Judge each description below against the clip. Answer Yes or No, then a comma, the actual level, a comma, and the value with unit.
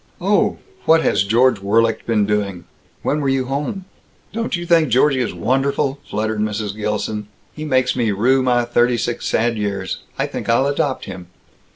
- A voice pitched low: Yes, low, 120 Hz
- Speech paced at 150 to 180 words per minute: Yes, average, 175 wpm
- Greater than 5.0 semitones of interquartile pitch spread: No, average, 4.3 semitones